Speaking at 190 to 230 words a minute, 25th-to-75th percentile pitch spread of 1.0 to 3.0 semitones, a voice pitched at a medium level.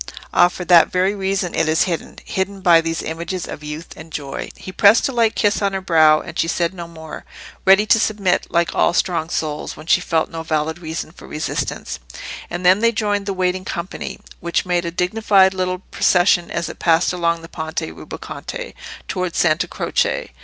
Yes: average, 195 wpm; narrow, 2.6 semitones; medium, 175 Hz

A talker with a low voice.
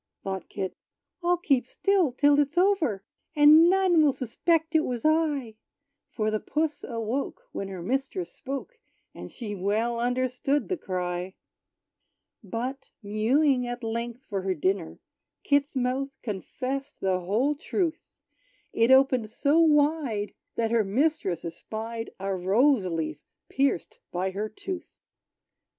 No: very high, 250 Hz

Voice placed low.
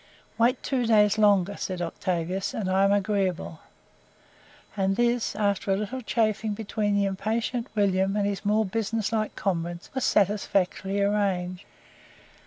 No: high, 200 Hz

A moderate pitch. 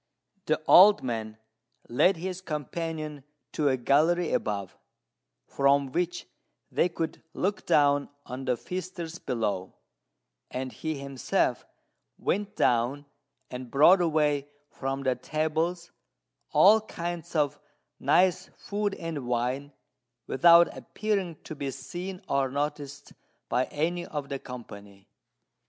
Yes: medium, 150 Hz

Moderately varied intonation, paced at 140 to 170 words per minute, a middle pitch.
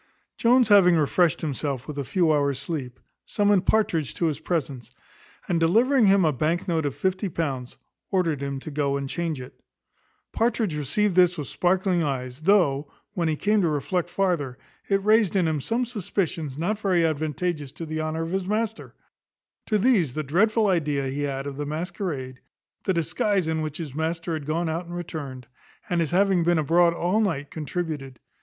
No: average, 4.4 semitones; average, 185 wpm; medium, 165 Hz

